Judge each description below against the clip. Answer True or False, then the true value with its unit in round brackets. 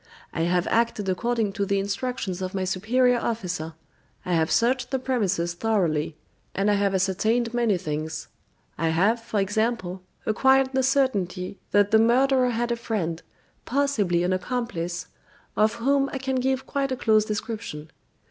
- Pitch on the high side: True (215 Hz)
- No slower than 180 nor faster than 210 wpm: False (155 wpm)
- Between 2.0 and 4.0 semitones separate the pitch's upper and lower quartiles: False (5.1 semitones)